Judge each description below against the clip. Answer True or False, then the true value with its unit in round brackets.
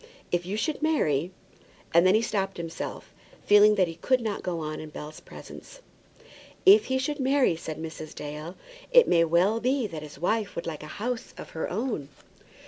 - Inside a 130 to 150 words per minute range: False (195 wpm)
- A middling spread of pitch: False (6.7 semitones)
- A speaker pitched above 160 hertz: True (185 Hz)